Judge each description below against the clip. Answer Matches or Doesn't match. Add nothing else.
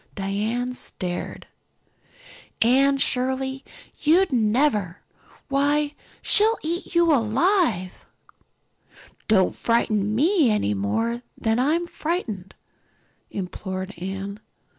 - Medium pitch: Doesn't match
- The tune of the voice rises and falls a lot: Matches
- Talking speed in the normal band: Doesn't match